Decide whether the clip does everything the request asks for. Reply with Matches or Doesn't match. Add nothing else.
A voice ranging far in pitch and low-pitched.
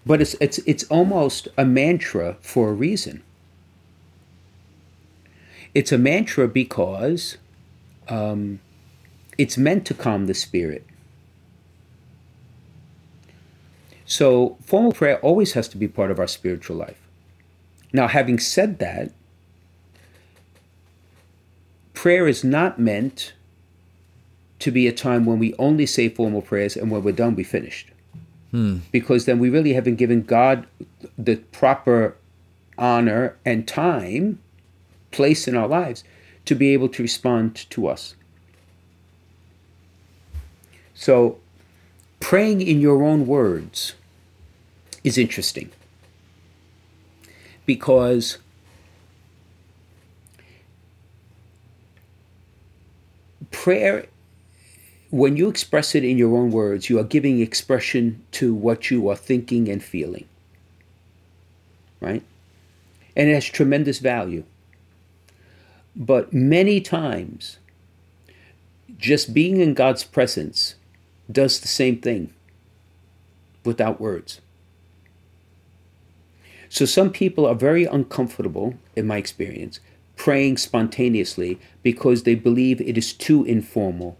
Matches